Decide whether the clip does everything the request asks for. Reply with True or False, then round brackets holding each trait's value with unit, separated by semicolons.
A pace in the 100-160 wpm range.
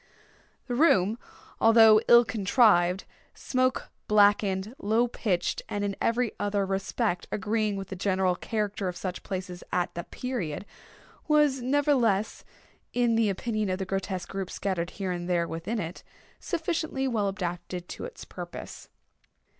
True (140 wpm)